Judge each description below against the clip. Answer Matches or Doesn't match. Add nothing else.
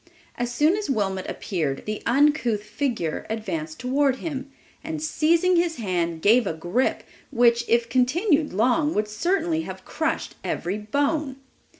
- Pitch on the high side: Matches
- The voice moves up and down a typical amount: Doesn't match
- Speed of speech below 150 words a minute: Matches